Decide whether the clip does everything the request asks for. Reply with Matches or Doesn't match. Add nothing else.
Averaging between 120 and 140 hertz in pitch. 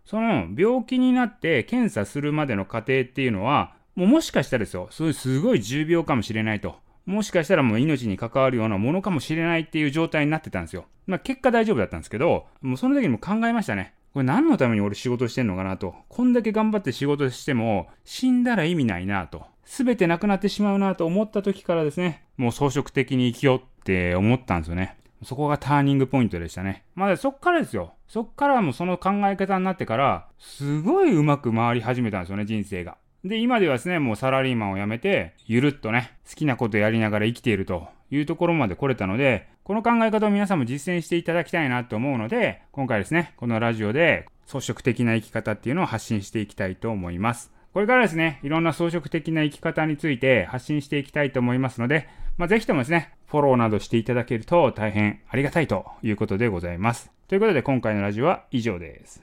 Matches